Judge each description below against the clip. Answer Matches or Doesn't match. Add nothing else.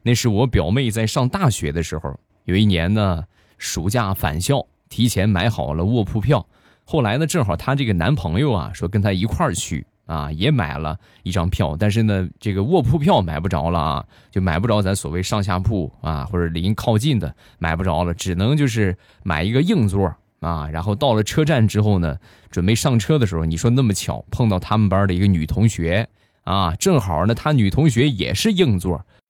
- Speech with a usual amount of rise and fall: Matches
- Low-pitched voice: Matches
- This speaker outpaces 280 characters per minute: Matches